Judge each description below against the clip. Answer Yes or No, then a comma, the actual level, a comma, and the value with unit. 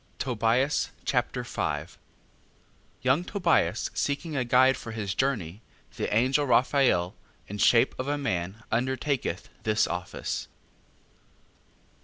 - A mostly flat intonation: No, average, 4.4 semitones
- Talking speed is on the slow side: Yes, slow, 110 wpm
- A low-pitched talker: Yes, low, 125 Hz